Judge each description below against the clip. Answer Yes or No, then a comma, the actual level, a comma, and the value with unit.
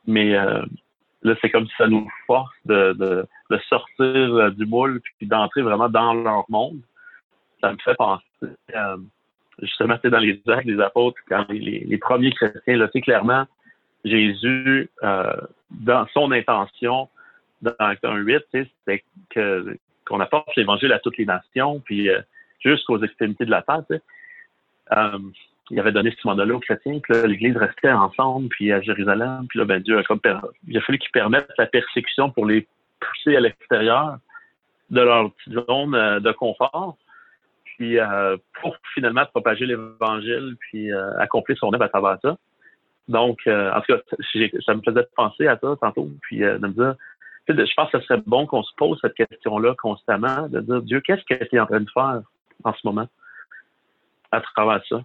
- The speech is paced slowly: No, average, 185 wpm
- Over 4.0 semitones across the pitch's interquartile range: No, average, 3.6 semitones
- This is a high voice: No, low, 115 Hz